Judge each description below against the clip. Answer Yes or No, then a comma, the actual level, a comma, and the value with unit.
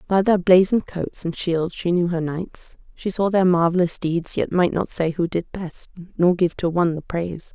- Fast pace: Yes, fast, 225 wpm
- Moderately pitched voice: Yes, medium, 175 Hz